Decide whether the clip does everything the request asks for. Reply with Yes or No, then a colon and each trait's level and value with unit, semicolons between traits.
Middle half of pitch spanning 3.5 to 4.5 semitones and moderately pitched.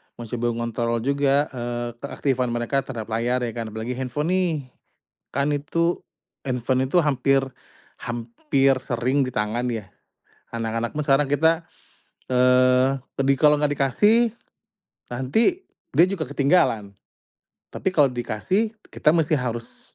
No: average, 3.8 semitones; low, 130 Hz